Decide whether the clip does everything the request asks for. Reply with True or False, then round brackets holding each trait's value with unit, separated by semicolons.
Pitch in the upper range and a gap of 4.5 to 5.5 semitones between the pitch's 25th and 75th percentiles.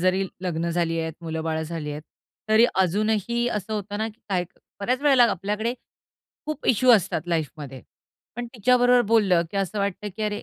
True (200 Hz; 4.9 semitones)